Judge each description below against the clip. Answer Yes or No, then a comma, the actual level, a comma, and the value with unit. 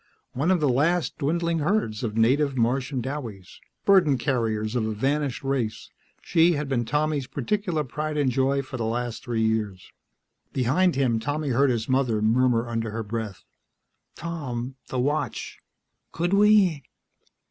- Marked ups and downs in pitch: No, average, 4.7 semitones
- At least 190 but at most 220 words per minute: No, average, 150 wpm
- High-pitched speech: No, low, 130 Hz